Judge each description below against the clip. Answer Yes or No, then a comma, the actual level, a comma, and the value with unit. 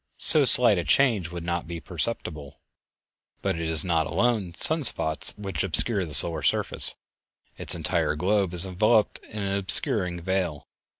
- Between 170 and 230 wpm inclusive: No, average, 160 wpm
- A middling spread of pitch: Yes, average, 4.1 semitones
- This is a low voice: Yes, very low, 90 Hz